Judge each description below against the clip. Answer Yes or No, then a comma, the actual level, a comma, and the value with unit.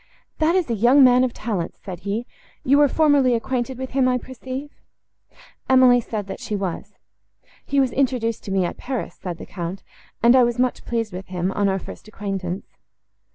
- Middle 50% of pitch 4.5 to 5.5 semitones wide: Yes, average, 4.9 semitones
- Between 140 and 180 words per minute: No, average, 195 wpm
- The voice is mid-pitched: No, high, 240 Hz